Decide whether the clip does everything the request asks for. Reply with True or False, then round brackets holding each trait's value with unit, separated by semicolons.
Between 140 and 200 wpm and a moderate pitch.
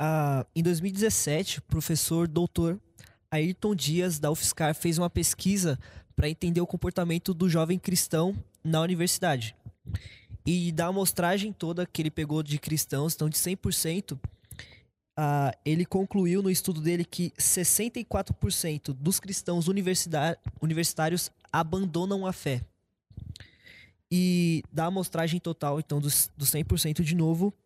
False (125 wpm; 165 Hz)